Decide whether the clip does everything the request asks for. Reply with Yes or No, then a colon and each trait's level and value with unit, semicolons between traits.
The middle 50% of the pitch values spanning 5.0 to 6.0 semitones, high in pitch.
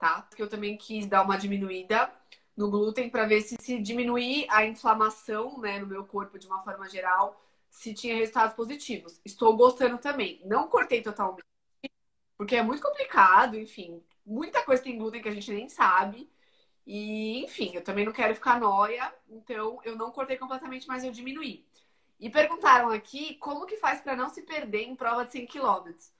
No: average, 3.8 semitones; high, 225 Hz